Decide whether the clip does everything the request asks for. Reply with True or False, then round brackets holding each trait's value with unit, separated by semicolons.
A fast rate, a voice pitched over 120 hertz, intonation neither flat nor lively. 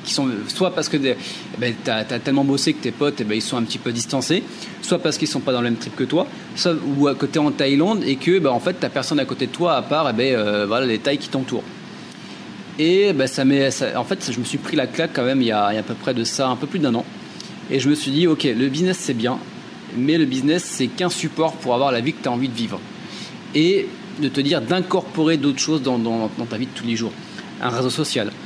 True (290 wpm; 140 Hz; 4.6 semitones)